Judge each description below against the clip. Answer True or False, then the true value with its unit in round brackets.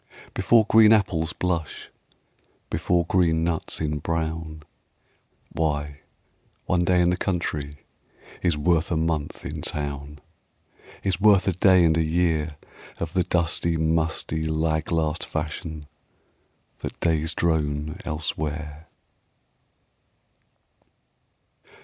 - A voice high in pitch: False (80 Hz)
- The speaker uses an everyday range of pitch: False (2.0 semitones)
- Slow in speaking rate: True (105 wpm)